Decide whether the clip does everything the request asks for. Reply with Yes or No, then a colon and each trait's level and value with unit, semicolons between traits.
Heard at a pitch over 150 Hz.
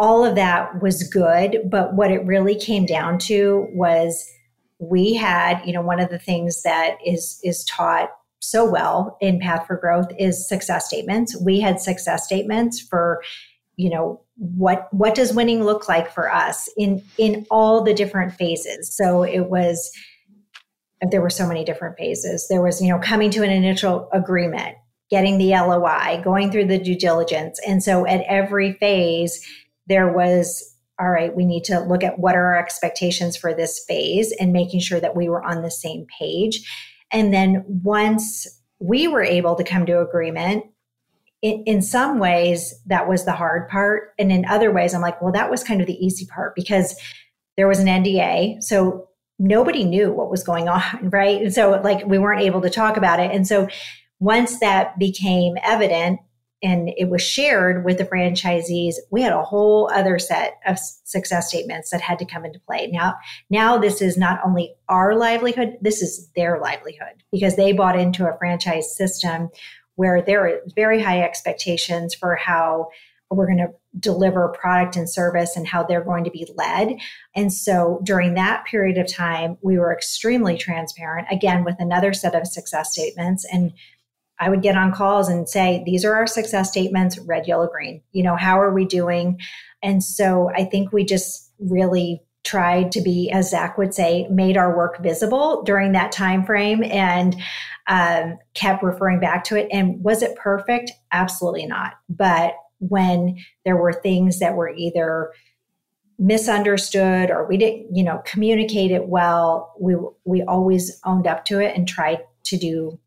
Yes: medium, 185 Hz